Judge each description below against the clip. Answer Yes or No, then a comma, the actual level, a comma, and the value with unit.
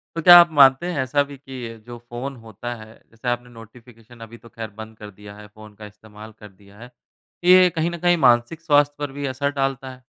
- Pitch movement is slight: No, average, 4.4 semitones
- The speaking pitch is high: No, low, 120 Hz